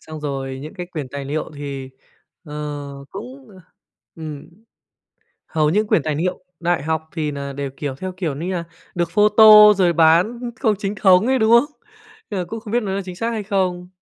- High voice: No, medium, 175 Hz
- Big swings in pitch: Yes, wide, 5.8 semitones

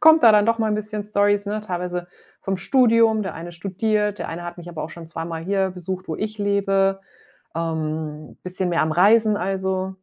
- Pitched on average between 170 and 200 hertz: Yes, high, 190 Hz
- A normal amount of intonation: Yes, average, 3.4 semitones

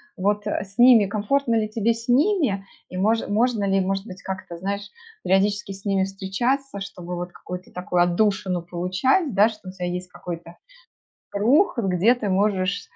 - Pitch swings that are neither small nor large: Yes, average, 3.3 semitones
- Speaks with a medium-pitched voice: No, high, 200 Hz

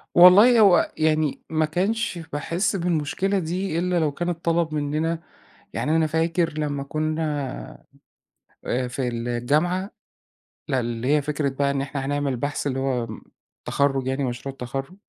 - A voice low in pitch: No, medium, 150 Hz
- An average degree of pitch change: Yes, average, 4.0 semitones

